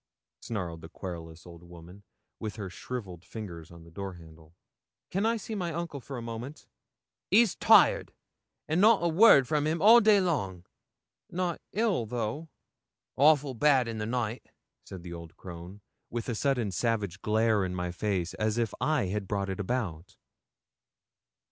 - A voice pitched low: Yes, low, 110 Hz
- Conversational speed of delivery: Yes, average, 165 wpm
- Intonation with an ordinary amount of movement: No, wide, 8.5 semitones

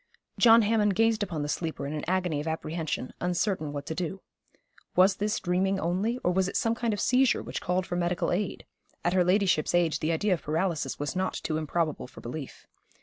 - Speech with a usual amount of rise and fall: Yes, average, 3.7 semitones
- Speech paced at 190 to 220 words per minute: Yes, fast, 205 wpm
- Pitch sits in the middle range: Yes, medium, 180 Hz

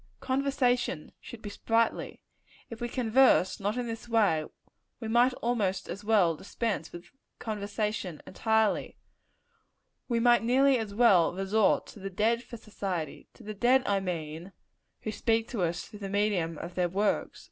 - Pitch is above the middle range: Yes, high, 215 Hz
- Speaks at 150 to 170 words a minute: Yes, average, 160 wpm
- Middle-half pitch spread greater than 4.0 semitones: No, average, 3.6 semitones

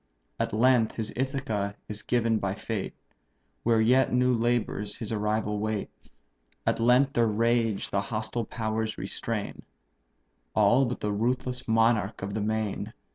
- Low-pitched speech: Yes, low, 110 Hz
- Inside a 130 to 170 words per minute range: Yes, average, 140 wpm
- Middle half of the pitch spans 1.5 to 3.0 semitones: Yes, narrow, 2.4 semitones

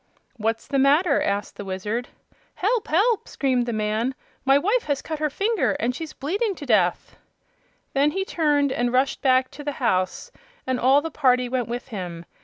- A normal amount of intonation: Yes, average, 4.5 semitones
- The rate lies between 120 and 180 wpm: No, average, 190 wpm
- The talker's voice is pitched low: No, very high, 265 Hz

